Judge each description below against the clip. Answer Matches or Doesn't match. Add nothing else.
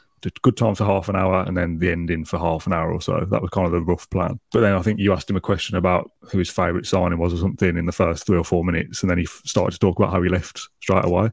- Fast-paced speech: Matches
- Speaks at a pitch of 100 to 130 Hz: Doesn't match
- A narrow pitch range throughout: Matches